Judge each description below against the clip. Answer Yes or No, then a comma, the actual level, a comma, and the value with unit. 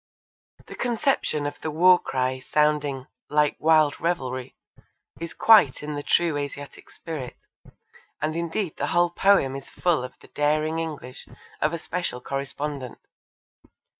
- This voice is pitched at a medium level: Yes, medium, 150 Hz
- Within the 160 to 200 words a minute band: No, slow, 135 wpm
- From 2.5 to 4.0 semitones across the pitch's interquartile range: Yes, average, 3.4 semitones